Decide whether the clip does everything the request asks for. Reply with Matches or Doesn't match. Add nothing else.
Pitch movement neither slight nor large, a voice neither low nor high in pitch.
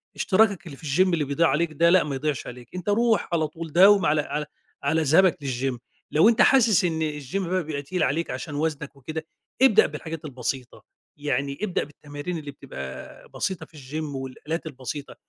Matches